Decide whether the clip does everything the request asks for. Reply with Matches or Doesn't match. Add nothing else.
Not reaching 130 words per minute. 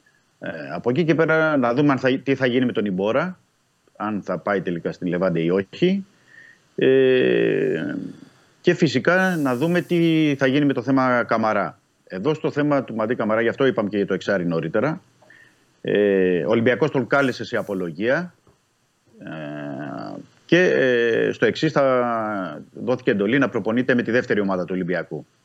Doesn't match